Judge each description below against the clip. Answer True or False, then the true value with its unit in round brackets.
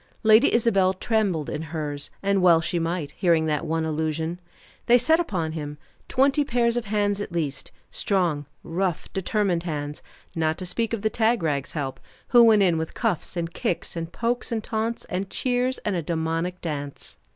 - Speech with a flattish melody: False (5.4 semitones)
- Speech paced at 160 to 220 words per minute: True (175 wpm)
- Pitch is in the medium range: True (180 Hz)